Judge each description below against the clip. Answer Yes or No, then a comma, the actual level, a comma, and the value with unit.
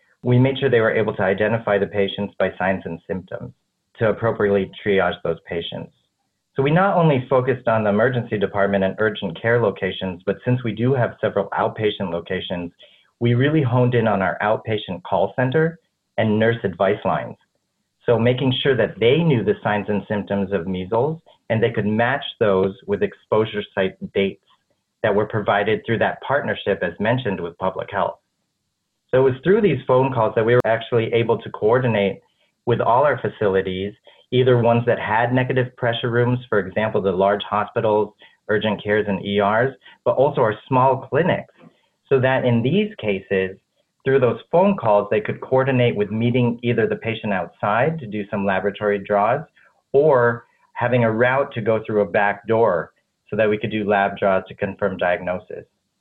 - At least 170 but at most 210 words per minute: Yes, average, 180 wpm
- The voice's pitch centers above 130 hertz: No, low, 110 Hz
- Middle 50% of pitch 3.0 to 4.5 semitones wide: Yes, average, 3.6 semitones